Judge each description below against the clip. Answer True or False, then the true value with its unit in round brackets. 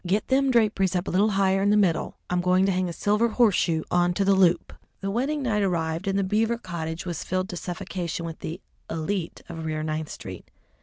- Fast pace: True (220 wpm)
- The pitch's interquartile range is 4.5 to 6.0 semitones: False (3.1 semitones)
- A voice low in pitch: False (185 Hz)